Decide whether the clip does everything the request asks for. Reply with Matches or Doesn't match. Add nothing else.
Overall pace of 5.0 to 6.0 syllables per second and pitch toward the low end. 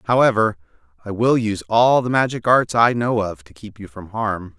Matches